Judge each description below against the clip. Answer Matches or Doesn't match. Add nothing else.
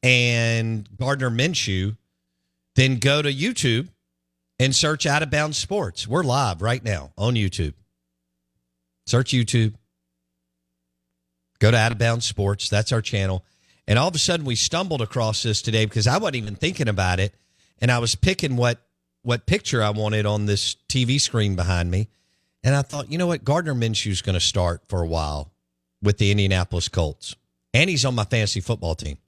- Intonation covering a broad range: Matches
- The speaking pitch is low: Matches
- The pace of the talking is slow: Doesn't match